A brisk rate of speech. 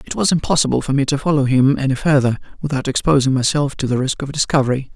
Yes: fast, 220 wpm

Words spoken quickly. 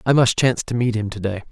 Yes: fast, 320 wpm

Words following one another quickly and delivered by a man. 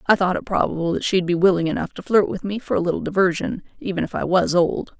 No: fast, 265 wpm; female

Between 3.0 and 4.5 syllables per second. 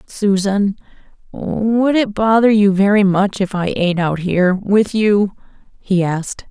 Yes: 4.1 syllables/s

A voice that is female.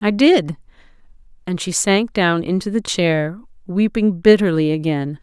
Yes: female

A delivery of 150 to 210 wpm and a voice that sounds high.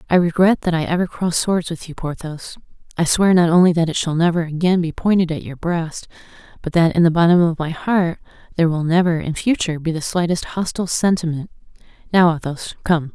No: fast, 205 wpm; medium, 170 Hz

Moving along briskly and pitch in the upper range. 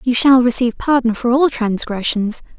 No: average, 160 wpm; high, 245 Hz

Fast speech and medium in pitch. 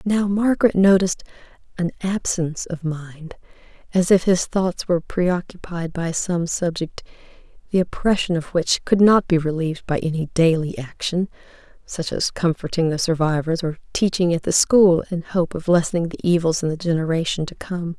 No: average, 170 wpm; medium, 175 Hz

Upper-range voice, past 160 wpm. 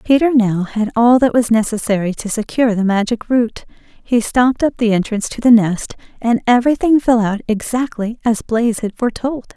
Yes: high, 230 Hz; average, 180 wpm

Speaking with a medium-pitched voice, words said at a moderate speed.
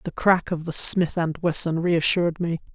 Yes: medium, 170 Hz; average, 195 wpm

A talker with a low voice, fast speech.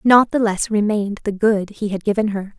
No: high, 210 Hz; fast, 230 wpm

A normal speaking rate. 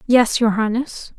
Yes: average, 150 wpm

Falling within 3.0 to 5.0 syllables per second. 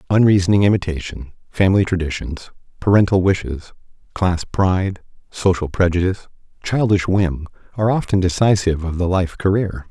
No: 5.5 syllables/s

